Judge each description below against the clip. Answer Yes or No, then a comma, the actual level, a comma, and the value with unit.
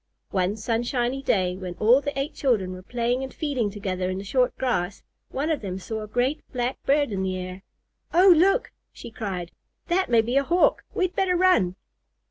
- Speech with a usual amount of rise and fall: No, wide, 6.8 semitones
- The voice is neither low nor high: No, high, 240 Hz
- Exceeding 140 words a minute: Yes, average, 195 wpm